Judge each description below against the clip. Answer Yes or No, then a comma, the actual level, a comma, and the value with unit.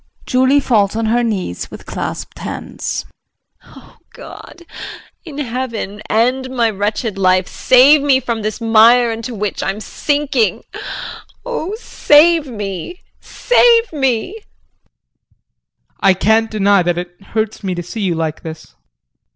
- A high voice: Yes, high, 225 Hz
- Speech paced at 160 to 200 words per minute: No, slow, 135 wpm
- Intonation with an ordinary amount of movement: Yes, average, 4.8 semitones